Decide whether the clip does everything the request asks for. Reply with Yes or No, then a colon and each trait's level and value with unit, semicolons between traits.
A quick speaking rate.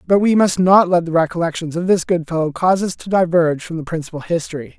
Yes: fast, 240 wpm